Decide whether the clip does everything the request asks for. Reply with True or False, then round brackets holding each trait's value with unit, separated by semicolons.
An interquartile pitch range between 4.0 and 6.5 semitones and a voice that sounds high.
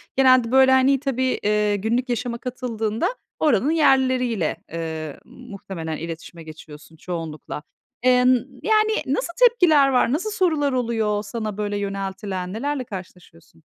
True (5.6 semitones; 235 Hz)